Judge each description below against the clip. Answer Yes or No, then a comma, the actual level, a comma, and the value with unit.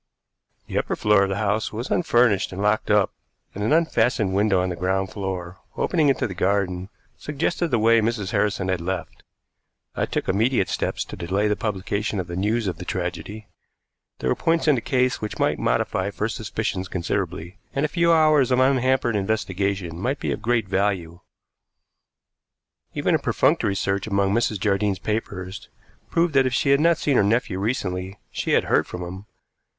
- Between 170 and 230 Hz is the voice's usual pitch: No, low, 105 Hz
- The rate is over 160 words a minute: Yes, average, 185 wpm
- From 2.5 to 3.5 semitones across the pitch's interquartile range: No, average, 4.1 semitones